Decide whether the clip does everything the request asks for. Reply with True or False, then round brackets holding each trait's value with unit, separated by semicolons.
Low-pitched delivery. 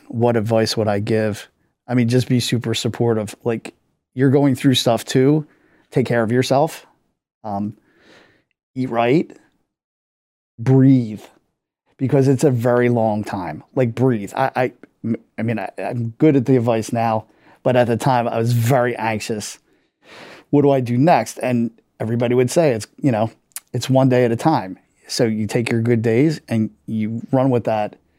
True (120 Hz)